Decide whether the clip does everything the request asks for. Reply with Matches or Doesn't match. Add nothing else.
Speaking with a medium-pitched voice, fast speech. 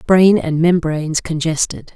Doesn't match